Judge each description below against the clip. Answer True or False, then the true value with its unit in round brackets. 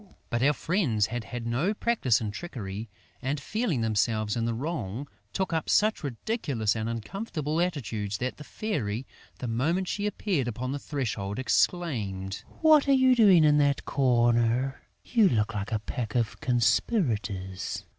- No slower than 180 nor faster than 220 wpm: False (155 wpm)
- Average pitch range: False (7.5 semitones)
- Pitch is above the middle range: False (125 Hz)